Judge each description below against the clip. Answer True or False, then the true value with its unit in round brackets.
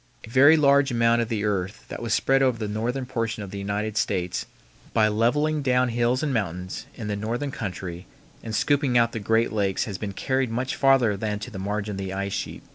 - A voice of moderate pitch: False (115 Hz)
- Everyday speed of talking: False (220 wpm)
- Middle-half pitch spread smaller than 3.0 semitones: False (3.8 semitones)